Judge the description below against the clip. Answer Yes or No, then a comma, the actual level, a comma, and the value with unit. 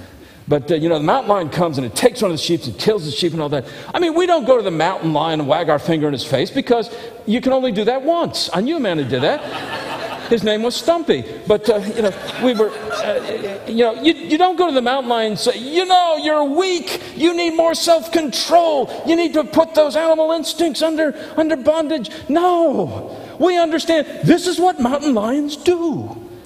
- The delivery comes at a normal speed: No, fast, 225 wpm